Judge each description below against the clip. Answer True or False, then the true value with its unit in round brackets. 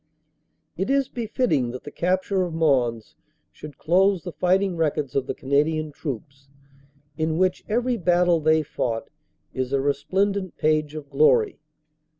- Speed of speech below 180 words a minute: True (145 wpm)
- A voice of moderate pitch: True (160 Hz)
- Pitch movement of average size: True (4.9 semitones)